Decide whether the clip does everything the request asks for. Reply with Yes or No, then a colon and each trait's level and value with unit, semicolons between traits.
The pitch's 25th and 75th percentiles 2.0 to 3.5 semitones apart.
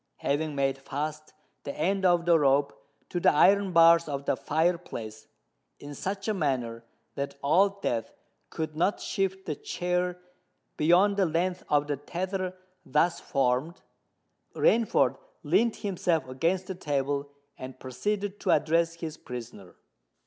No: average, 4.7 semitones